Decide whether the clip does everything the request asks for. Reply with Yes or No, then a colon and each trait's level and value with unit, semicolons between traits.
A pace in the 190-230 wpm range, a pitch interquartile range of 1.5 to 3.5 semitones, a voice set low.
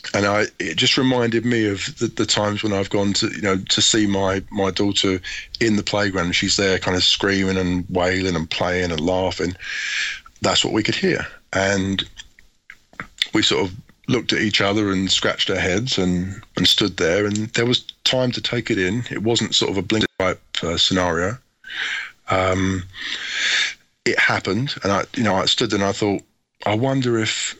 Yes: average, 195 wpm; average, 2.9 semitones; low, 100 Hz